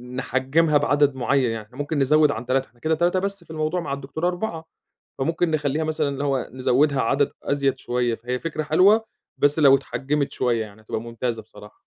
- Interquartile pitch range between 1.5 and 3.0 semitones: No, average, 3.7 semitones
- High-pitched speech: No, medium, 140 Hz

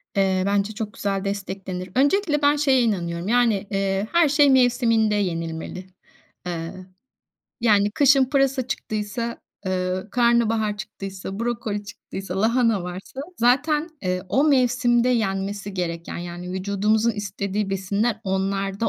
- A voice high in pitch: Yes, high, 205 Hz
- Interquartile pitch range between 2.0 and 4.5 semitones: Yes, average, 3.9 semitones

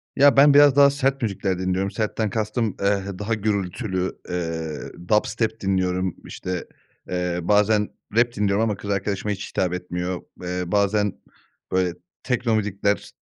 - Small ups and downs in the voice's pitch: No, average, 3.1 semitones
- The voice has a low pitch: Yes, low, 100 Hz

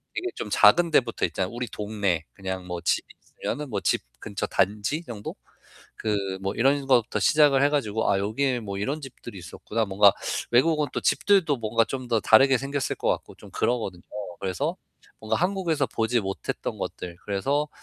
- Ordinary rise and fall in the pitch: No, wide, 5.7 semitones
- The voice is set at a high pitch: No, low, 115 Hz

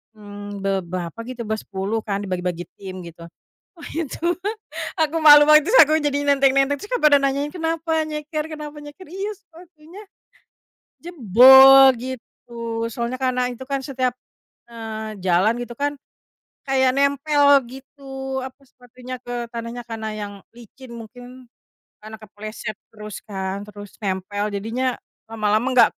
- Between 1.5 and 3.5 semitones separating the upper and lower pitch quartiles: No, average, 5.0 semitones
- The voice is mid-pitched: No, very high, 255 Hz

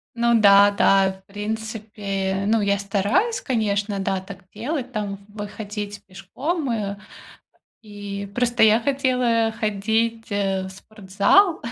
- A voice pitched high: Yes, high, 210 Hz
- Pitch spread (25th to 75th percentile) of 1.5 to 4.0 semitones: Yes, narrow, 2.5 semitones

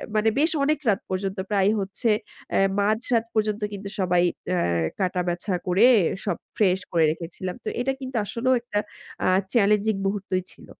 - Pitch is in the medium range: No, high, 200 Hz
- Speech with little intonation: No, average, 3.1 semitones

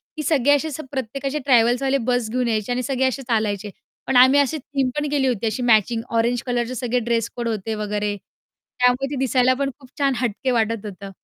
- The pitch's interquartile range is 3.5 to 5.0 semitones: No, average, 3.1 semitones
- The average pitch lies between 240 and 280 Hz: Yes, very high, 250 Hz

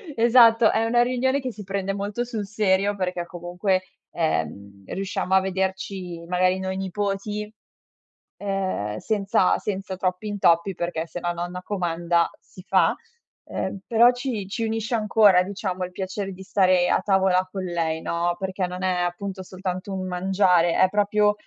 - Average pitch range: No, narrow, 2.3 semitones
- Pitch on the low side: No, high, 190 Hz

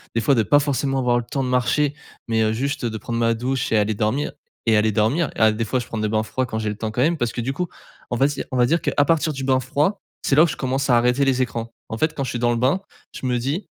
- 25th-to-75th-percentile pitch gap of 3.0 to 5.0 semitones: Yes, average, 3.4 semitones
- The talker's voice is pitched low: Yes, low, 125 Hz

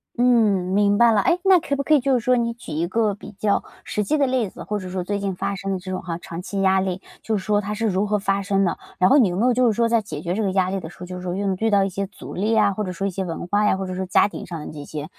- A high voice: Yes, high, 200 Hz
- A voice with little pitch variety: No, average, 3.1 semitones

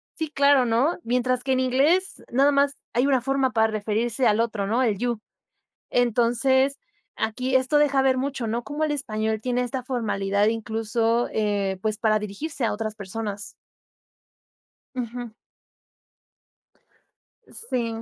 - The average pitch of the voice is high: Yes, high, 240 Hz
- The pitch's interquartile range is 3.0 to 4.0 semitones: Yes, average, 3.3 semitones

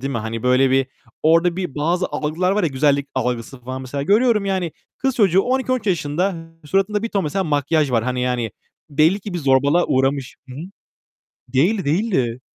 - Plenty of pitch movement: Yes, wide, 6.3 semitones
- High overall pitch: No, medium, 150 Hz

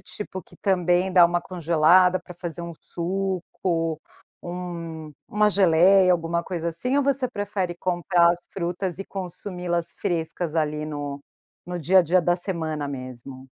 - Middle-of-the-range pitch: Yes, medium, 175 Hz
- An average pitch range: No, narrow, 2.2 semitones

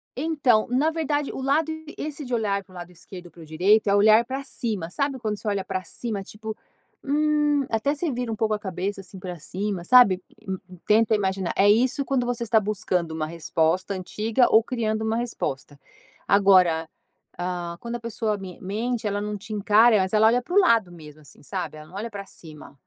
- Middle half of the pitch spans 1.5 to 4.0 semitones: No, average, 4.6 semitones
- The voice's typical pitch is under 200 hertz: No, high, 210 Hz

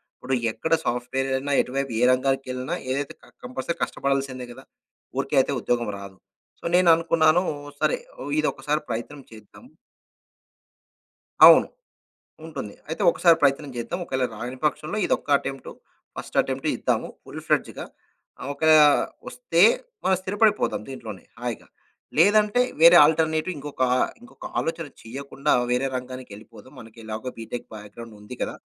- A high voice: No, low, 135 Hz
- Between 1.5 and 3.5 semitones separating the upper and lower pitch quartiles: No, average, 4.6 semitones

